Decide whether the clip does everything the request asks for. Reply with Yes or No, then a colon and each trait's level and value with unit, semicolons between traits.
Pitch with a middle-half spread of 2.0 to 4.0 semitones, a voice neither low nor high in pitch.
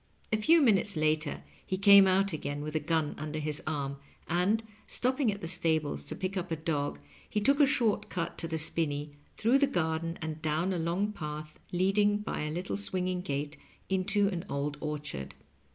No: average, 4.6 semitones; medium, 170 Hz